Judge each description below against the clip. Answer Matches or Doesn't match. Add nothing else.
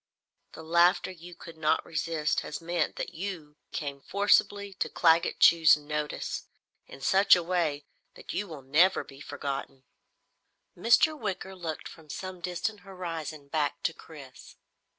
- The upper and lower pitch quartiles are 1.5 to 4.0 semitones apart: Matches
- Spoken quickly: Doesn't match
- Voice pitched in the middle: Matches